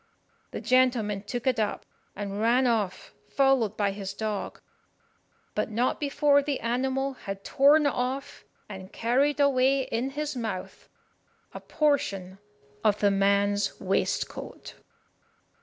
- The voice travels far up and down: No, average, 5.0 semitones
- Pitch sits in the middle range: No, high, 235 Hz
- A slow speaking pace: Yes, slow, 125 wpm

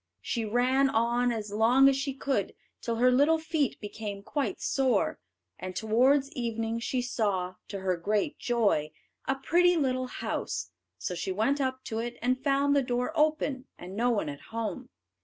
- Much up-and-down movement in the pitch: No, average, 3.8 semitones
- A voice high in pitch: Yes, high, 245 Hz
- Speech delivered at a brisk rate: No, average, 175 wpm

